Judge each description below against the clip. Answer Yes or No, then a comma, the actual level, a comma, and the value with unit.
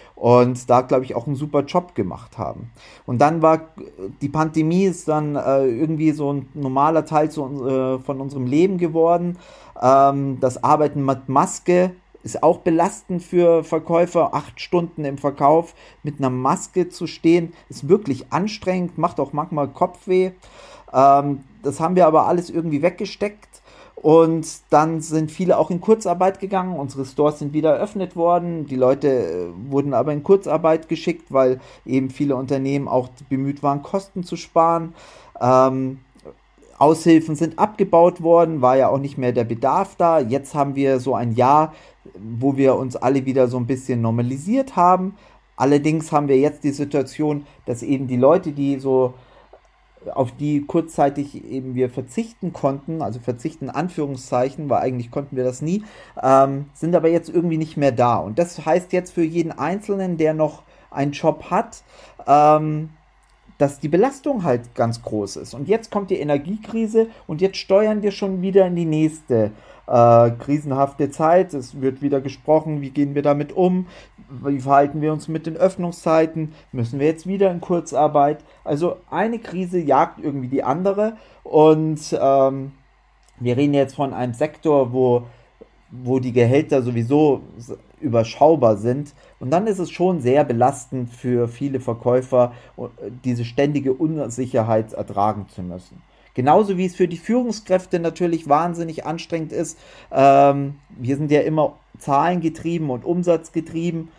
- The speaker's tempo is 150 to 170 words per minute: Yes, average, 160 wpm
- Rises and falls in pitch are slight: No, average, 4.2 semitones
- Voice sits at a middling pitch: Yes, medium, 150 Hz